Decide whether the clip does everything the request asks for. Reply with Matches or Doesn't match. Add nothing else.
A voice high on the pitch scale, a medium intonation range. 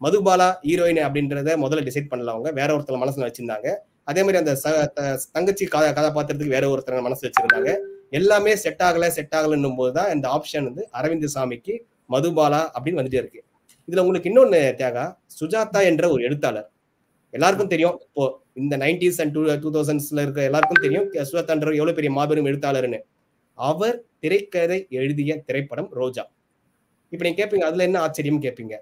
Doesn't match